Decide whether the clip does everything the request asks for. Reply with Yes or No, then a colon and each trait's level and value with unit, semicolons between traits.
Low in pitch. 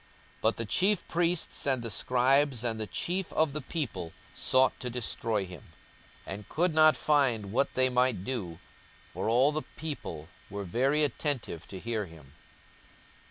Yes: low, 125 Hz